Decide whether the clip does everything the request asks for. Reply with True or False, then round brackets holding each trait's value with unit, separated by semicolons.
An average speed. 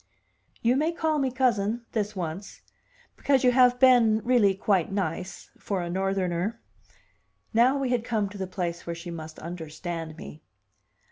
True (160 wpm)